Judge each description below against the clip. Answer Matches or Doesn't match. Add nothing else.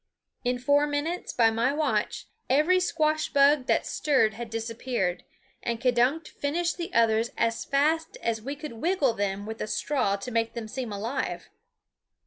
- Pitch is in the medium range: Doesn't match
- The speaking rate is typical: Matches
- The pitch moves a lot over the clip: Doesn't match